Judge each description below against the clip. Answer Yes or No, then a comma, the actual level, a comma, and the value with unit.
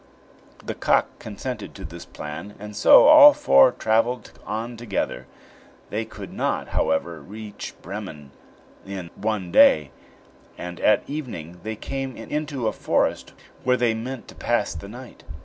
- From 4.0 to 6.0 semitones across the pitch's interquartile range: Yes, wide, 5.5 semitones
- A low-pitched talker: Yes, low, 105 Hz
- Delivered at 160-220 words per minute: No, average, 145 wpm